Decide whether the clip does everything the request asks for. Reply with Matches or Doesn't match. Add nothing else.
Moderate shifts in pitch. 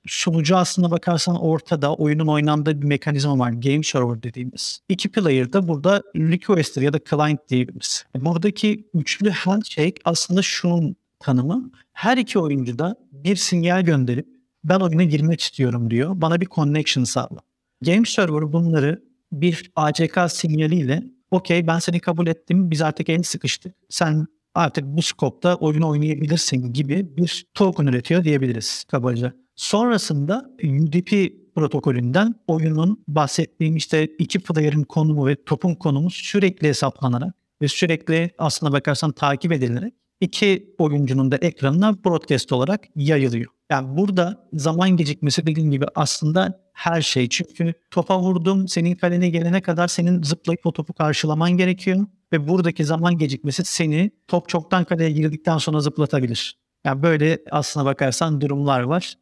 Matches